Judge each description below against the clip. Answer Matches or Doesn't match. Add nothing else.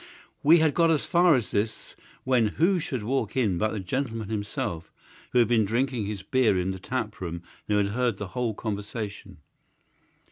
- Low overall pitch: Matches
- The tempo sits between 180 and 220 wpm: Matches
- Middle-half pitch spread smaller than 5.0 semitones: Matches